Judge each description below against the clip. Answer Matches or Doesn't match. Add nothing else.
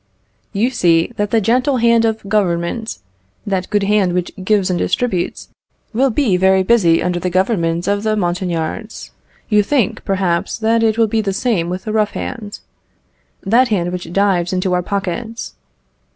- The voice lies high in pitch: Matches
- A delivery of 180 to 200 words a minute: Doesn't match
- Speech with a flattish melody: Doesn't match